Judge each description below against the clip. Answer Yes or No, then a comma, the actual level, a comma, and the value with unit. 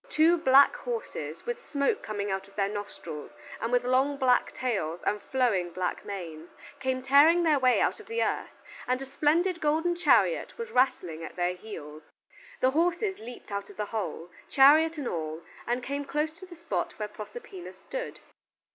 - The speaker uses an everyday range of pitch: No, wide, 8.2 semitones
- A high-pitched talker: Yes, very high, 260 Hz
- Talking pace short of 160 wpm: No, average, 180 wpm